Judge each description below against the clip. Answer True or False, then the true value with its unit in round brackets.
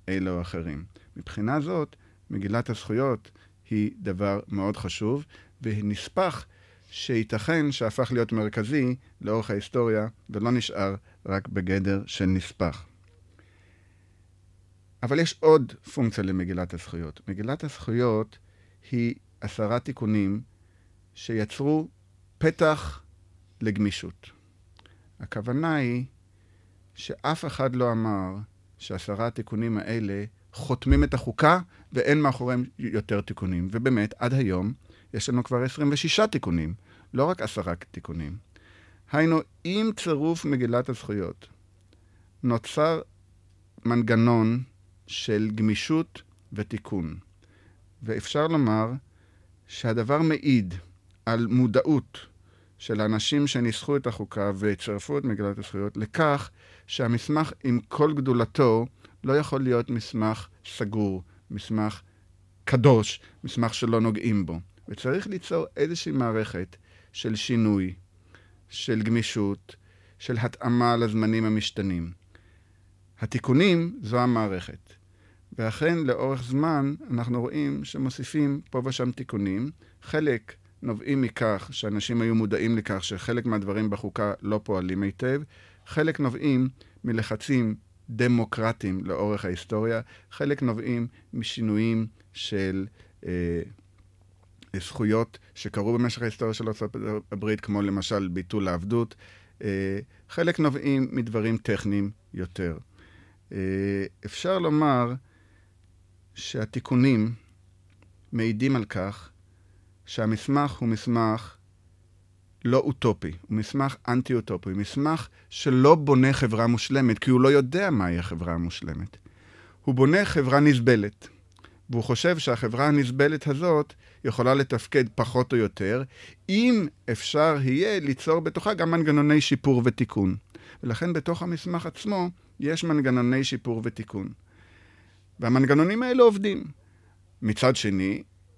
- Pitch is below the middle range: True (110 Hz)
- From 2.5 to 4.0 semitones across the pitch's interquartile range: False (5.0 semitones)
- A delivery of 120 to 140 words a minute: False (100 wpm)